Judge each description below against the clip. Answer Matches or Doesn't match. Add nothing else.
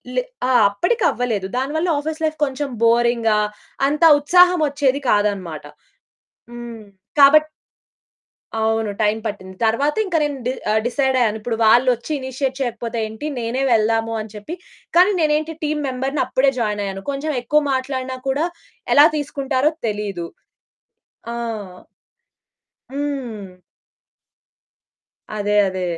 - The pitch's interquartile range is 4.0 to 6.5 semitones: Matches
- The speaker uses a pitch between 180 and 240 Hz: Doesn't match